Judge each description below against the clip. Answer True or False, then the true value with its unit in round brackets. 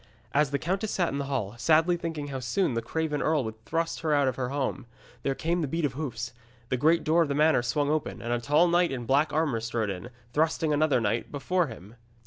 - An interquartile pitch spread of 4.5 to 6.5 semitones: True (4.8 semitones)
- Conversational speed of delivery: False (235 wpm)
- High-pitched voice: False (145 Hz)